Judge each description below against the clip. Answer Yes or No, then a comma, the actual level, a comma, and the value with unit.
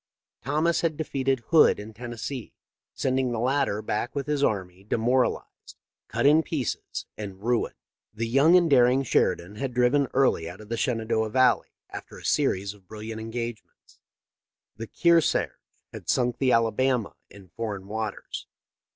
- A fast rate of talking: No, average, 165 wpm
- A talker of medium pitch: No, low, 120 Hz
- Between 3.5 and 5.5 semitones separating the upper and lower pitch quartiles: Yes, average, 3.9 semitones